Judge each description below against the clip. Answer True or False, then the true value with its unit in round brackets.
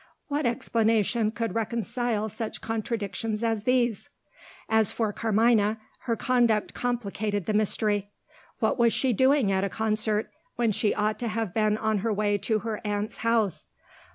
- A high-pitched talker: True (220 Hz)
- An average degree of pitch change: False (1.8 semitones)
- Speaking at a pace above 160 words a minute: False (155 wpm)